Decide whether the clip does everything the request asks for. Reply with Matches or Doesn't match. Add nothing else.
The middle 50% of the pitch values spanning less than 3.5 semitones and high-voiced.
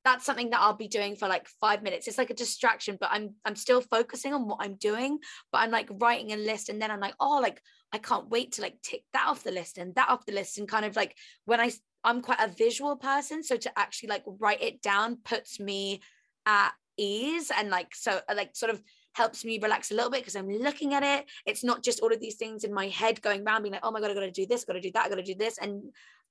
Matches